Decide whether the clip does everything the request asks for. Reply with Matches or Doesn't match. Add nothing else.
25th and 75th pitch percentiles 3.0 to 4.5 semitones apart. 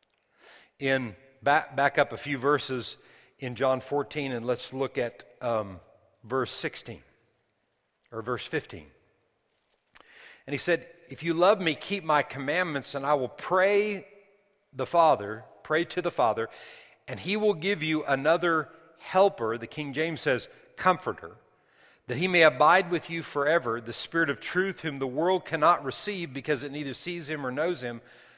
Doesn't match